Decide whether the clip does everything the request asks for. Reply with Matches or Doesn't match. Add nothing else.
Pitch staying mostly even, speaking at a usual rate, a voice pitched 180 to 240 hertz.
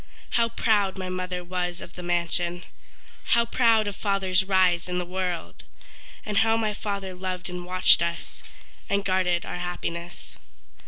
Matches